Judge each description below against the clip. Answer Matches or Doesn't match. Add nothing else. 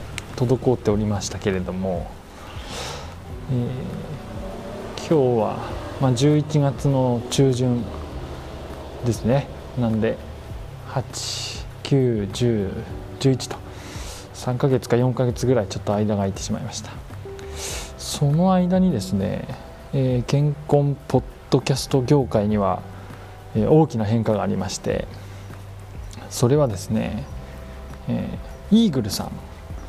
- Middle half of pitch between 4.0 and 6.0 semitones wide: Matches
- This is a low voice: Matches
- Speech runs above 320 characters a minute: Doesn't match